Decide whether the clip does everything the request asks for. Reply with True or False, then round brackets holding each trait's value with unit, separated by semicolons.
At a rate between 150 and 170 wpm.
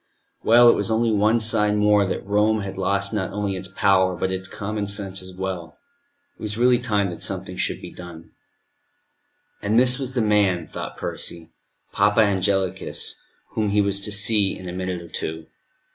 False (185 wpm)